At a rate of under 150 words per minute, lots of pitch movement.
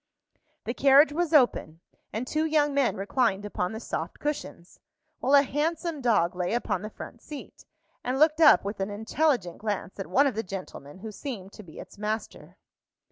No: average, 185 wpm; wide, 6.6 semitones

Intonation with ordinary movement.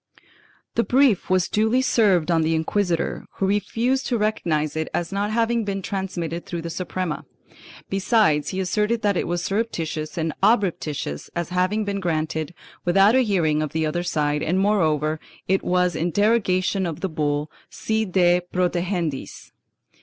Yes: average, 4.3 semitones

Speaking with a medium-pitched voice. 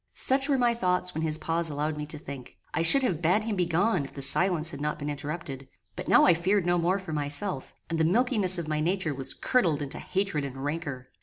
Yes: medium, 165 Hz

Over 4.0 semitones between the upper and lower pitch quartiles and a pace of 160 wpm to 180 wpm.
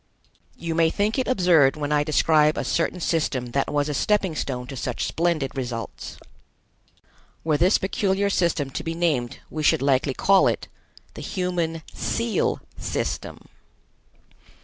No: average, 4.4 semitones; average, 150 wpm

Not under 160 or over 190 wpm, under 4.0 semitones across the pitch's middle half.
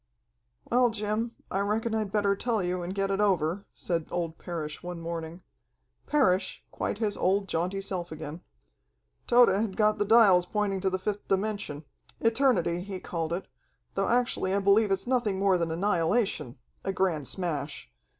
Yes: average, 165 wpm; average, 3.4 semitones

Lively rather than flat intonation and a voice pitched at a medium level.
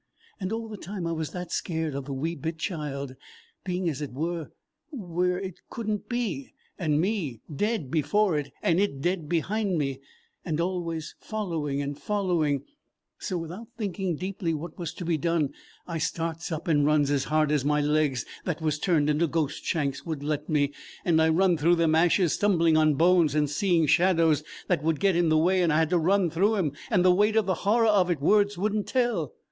No: average, 3.7 semitones; medium, 165 Hz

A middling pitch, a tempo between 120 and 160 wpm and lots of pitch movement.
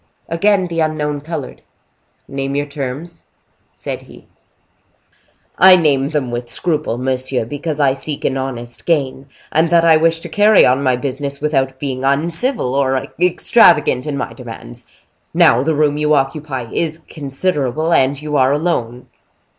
No: medium, 145 Hz; average, 150 wpm; average, 3.4 semitones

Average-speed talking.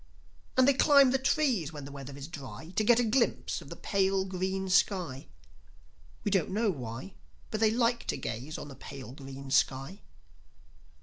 Yes: average, 180 wpm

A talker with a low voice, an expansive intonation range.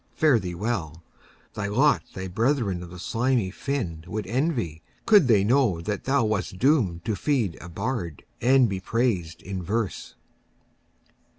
Yes: low, 105 Hz; wide, 6.0 semitones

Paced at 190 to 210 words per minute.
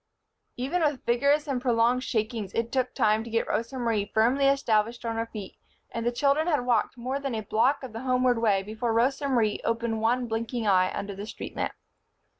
Yes: fast, 205 wpm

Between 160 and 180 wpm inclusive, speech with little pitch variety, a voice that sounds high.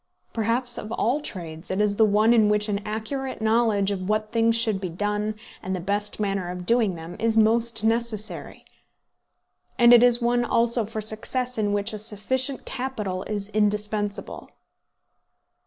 Yes: average, 165 wpm; narrow, 2.3 semitones; high, 215 Hz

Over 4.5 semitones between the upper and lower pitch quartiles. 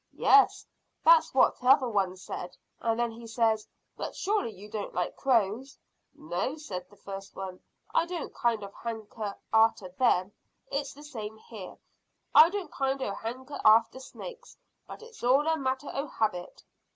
Yes: average, 5.2 semitones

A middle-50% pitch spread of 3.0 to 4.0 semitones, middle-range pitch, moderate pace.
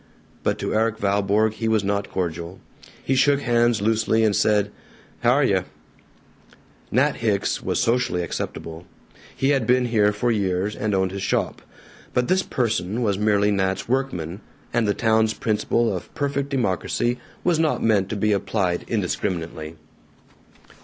No: average, 3.4 semitones; low, 110 Hz; average, 155 wpm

